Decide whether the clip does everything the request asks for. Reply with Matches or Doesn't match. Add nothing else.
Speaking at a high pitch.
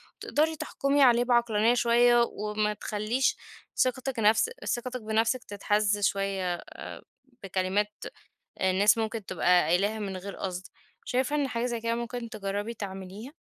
Matches